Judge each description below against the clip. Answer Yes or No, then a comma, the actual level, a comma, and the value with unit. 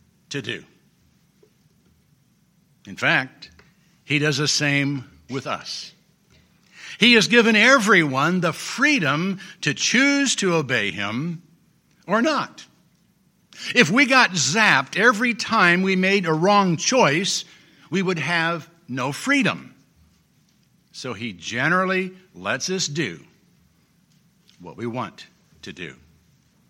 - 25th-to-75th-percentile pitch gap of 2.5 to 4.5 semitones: No, average, 5.3 semitones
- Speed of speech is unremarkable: No, slow, 110 wpm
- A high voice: No, medium, 175 Hz